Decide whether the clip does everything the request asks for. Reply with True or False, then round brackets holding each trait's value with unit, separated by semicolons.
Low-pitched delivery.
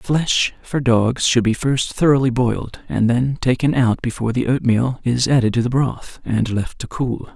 True (125 Hz)